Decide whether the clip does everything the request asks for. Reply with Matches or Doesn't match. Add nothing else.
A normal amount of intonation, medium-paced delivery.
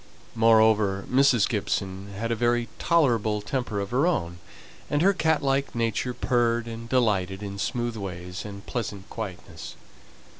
Matches